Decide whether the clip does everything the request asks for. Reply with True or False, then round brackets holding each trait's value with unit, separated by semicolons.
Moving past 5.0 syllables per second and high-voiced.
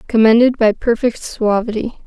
True (5.4 syllables/s; 225 Hz)